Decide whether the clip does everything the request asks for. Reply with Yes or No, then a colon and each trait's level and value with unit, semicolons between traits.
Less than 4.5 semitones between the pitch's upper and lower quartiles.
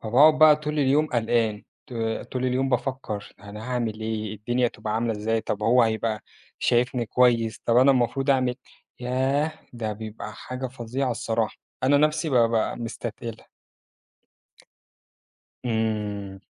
Yes: average, 3.0 semitones